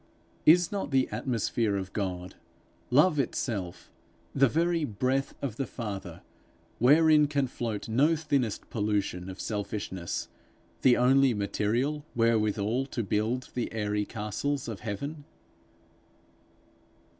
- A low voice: Yes, low, 120 Hz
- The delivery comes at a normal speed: No, slow, 115 wpm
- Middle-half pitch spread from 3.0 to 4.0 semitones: No, average, 5.2 semitones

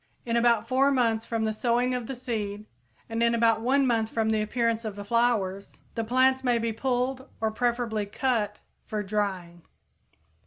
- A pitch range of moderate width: No, narrow, 2.3 semitones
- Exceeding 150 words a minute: Yes, average, 180 wpm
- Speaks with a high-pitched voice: Yes, high, 230 Hz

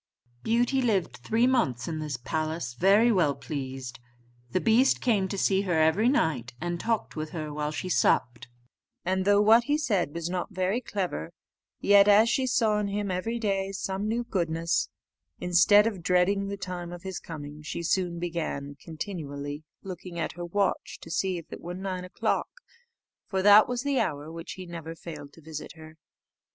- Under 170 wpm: No, average, 180 wpm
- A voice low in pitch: No, medium, 180 Hz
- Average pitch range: Yes, average, 4.5 semitones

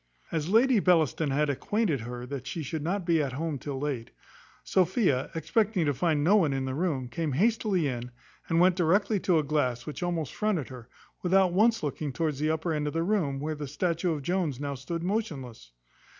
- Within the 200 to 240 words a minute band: Yes, fast, 205 wpm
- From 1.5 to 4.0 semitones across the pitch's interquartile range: No, average, 4.7 semitones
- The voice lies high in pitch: No, medium, 160 Hz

